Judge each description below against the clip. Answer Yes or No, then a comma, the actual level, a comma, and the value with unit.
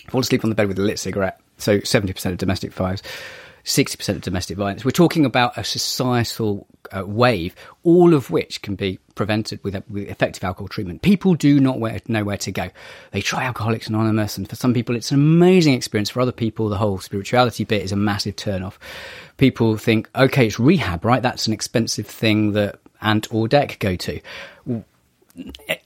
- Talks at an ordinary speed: Yes, average, 195 wpm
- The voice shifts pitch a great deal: No, average, 3.9 semitones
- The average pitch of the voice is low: Yes, low, 110 Hz